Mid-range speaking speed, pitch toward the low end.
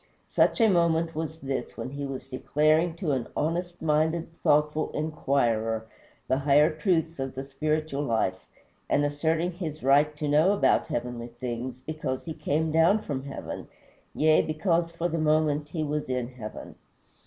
No: average, 160 wpm; medium, 150 Hz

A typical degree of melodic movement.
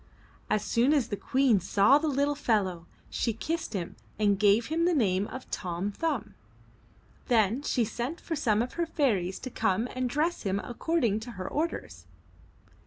No: wide, 6.1 semitones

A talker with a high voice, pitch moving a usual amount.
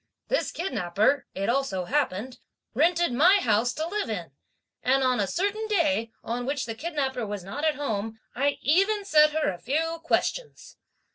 No: very high, 275 Hz; wide, 6.7 semitones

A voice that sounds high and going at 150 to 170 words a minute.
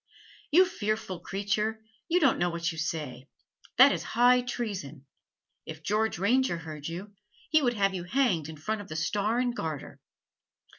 Yes: high, 200 Hz; average, 165 wpm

